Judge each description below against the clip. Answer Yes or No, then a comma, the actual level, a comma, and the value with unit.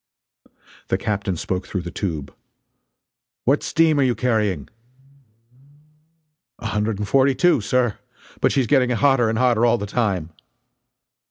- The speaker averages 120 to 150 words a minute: Yes, average, 140 wpm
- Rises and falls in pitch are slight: No, average, 4.2 semitones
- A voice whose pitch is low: Yes, low, 115 Hz